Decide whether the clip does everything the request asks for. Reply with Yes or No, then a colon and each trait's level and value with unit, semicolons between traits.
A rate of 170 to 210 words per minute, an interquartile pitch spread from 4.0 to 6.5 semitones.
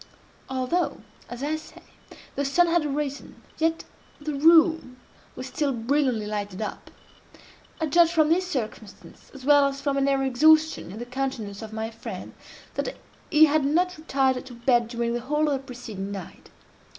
Yes: average, 175 wpm; average, 4.5 semitones